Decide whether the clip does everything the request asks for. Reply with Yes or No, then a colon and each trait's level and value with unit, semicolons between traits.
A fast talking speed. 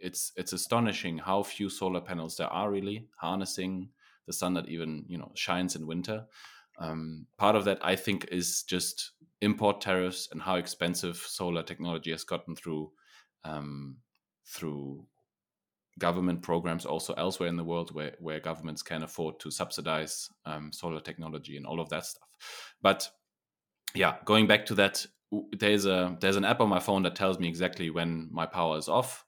No: average, 175 wpm